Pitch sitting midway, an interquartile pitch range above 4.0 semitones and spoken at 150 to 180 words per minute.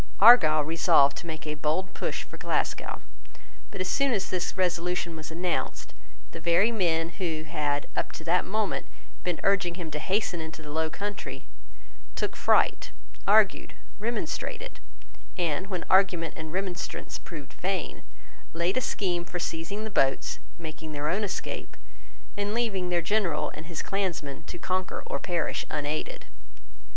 No: medium, 175 Hz; average, 3.5 semitones; average, 155 wpm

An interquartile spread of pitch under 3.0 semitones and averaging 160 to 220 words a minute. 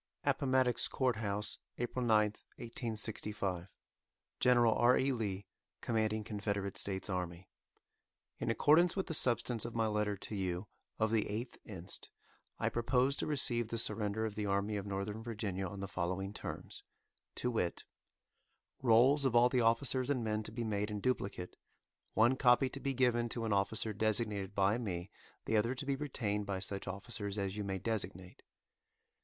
No: average, 3.3 semitones; average, 165 wpm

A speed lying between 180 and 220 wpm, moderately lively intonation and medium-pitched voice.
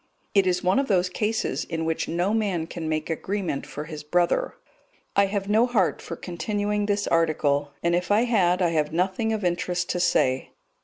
Yes: average, 195 wpm; average, 3.7 semitones; medium, 180 Hz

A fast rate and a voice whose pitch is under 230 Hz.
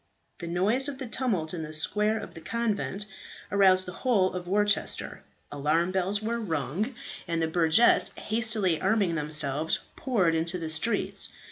No: average, 160 wpm; medium, 185 Hz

